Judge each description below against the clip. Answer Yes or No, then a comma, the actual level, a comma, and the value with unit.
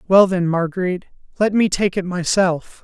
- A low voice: No, medium, 185 Hz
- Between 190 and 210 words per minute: No, average, 170 wpm